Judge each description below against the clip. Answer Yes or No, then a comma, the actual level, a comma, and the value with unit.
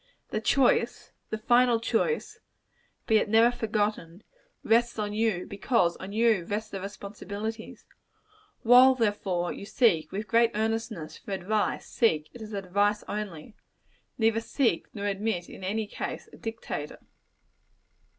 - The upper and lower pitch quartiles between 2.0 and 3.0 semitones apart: Yes, narrow, 2.5 semitones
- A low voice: No, high, 215 Hz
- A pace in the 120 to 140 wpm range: Yes, slow, 135 wpm